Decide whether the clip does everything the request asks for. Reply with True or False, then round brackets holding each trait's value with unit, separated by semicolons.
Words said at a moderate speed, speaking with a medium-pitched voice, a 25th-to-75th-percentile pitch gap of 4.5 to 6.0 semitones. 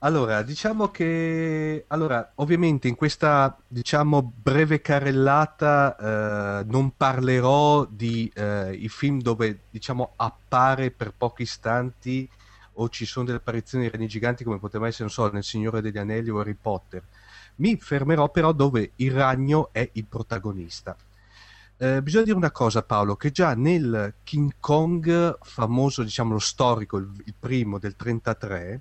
False (150 wpm; 120 Hz; 5.1 semitones)